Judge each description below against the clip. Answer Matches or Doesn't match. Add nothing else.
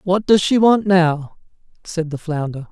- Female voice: Doesn't match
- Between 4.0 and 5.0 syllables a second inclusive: Matches